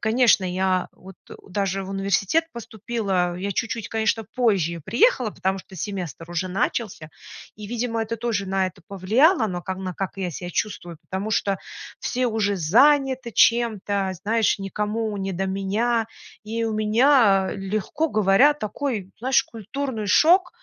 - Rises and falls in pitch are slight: No, average, 3.4 semitones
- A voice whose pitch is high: Yes, high, 210 Hz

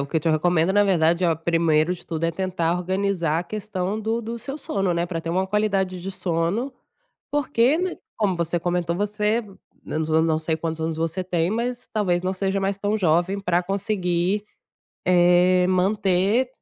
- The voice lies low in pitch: No, medium, 185 Hz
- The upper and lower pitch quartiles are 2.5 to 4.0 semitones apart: Yes, average, 3.3 semitones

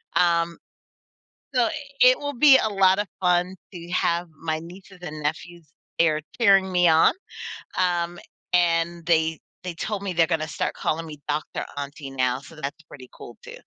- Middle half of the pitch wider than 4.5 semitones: No, average, 2.7 semitones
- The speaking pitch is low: No, medium, 170 Hz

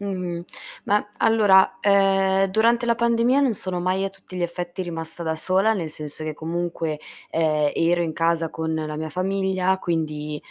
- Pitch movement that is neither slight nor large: Yes, average, 3.3 semitones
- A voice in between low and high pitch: Yes, medium, 180 Hz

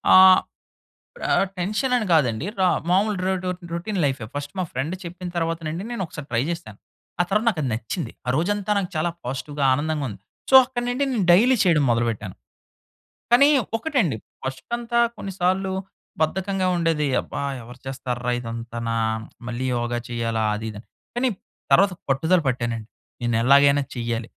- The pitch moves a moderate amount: No, wide, 8.0 semitones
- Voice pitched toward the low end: No, medium, 155 Hz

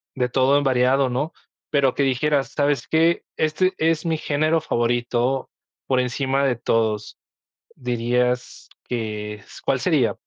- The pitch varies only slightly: No, average, 3.1 semitones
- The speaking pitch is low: Yes, low, 130 Hz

